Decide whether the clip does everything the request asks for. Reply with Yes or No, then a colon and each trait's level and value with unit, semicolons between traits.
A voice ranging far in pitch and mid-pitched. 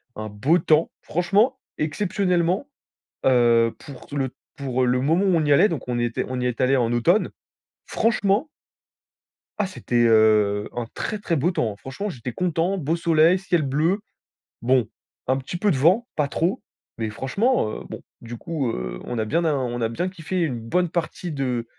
Yes: wide, 6.7 semitones; medium, 145 Hz